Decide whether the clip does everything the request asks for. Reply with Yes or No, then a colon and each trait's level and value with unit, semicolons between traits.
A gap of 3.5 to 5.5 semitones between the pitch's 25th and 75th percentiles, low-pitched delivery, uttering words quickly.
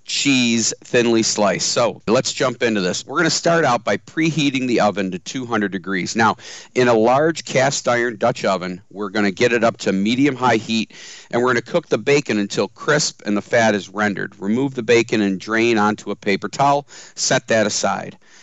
Yes: average, 4.8 semitones; low, 115 Hz; fast, 210 wpm